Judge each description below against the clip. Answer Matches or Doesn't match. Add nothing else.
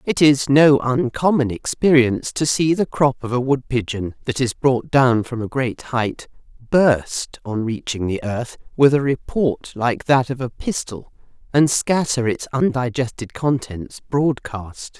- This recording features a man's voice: Doesn't match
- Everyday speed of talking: Matches